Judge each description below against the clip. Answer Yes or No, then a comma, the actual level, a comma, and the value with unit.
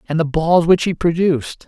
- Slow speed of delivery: No, fast, 215 wpm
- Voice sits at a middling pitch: Yes, medium, 165 Hz